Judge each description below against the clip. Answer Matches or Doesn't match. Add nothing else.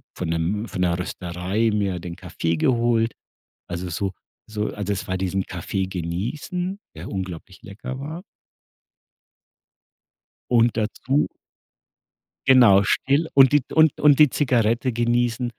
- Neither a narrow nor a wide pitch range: Doesn't match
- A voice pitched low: Matches